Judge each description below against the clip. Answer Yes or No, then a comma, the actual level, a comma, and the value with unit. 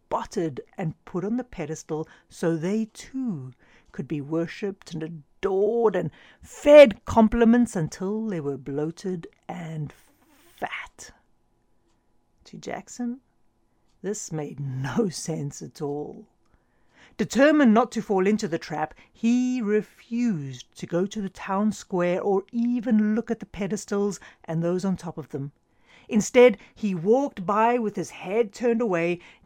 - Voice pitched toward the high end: Yes, high, 195 Hz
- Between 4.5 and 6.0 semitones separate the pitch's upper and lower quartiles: Yes, wide, 5.6 semitones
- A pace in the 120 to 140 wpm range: Yes, slow, 135 wpm